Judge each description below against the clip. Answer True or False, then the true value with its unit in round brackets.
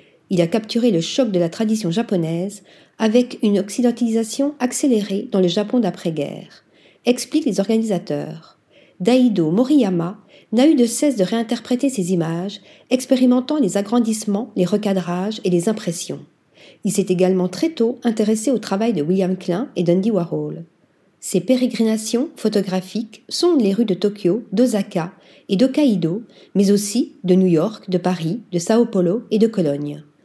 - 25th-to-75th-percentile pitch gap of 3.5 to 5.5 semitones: True (4.7 semitones)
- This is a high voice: True (210 Hz)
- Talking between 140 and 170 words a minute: True (150 wpm)